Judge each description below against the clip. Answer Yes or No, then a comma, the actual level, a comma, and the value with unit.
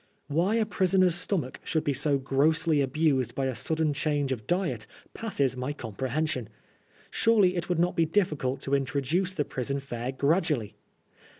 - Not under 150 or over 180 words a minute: Yes, average, 160 wpm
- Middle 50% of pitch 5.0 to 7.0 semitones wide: No, average, 4.6 semitones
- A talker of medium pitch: Yes, medium, 150 Hz